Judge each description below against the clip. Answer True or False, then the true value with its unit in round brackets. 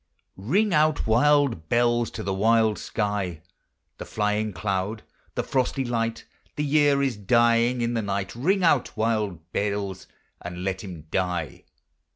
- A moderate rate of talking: True (150 wpm)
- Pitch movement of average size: True (4.1 semitones)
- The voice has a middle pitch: False (110 Hz)